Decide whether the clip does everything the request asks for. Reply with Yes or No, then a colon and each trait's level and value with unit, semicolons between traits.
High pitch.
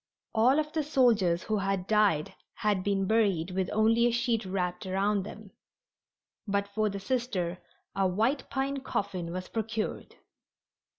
Yes: high, 205 Hz